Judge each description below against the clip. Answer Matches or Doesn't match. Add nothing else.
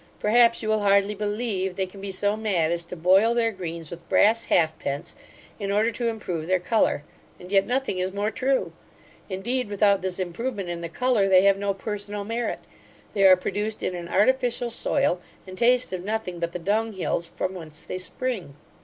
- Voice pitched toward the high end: Matches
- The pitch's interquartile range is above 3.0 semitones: Matches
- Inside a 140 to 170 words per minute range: Doesn't match